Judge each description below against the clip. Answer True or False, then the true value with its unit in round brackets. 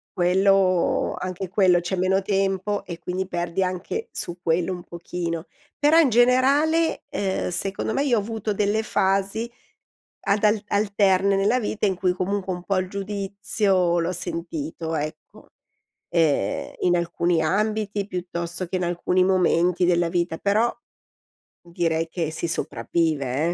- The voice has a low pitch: False (185 Hz)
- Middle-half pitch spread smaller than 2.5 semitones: False (2.8 semitones)